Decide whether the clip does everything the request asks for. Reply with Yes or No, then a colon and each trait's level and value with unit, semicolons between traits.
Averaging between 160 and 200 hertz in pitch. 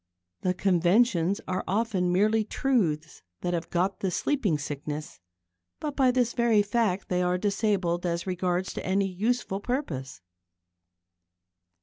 Yes: high, 190 Hz